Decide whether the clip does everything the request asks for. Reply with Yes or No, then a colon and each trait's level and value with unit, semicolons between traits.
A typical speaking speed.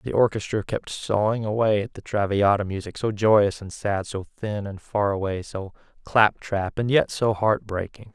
Yes: average, 190 wpm